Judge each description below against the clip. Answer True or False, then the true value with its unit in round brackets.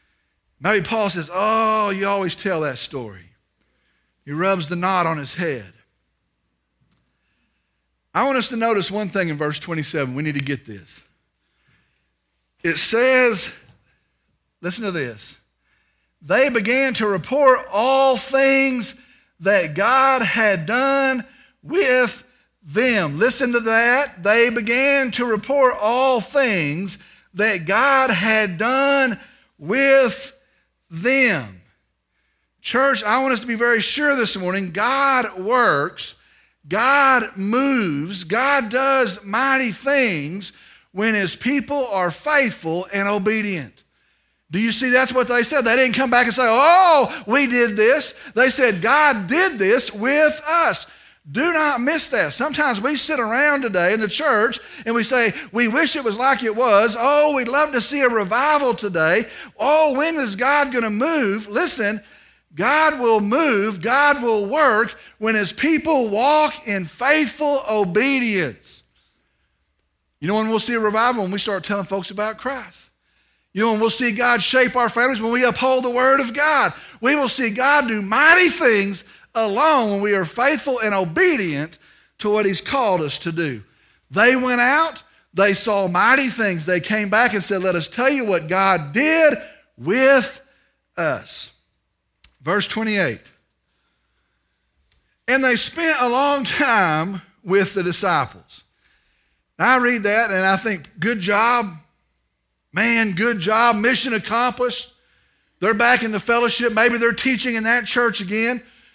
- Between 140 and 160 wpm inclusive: True (150 wpm)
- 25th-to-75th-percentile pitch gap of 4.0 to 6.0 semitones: True (5.5 semitones)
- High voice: True (230 Hz)